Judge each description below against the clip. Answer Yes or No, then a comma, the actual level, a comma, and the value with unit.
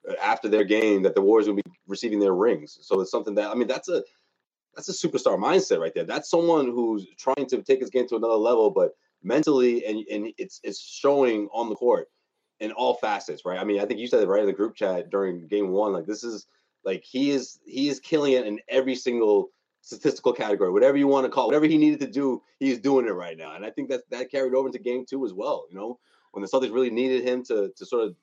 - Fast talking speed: Yes, fast, 255 wpm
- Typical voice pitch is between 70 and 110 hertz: No, medium, 140 Hz